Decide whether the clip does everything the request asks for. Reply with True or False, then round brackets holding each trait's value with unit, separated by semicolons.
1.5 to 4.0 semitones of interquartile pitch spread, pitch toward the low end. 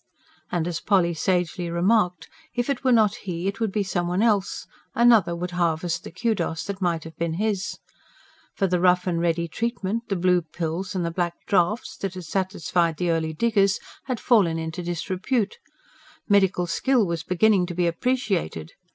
False (3.2 semitones; 180 Hz)